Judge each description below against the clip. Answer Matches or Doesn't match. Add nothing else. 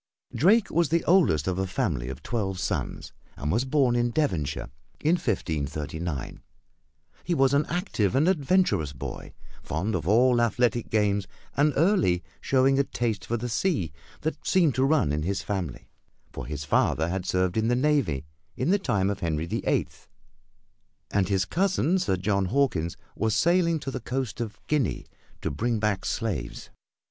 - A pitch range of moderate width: Doesn't match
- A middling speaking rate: Matches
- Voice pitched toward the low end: Matches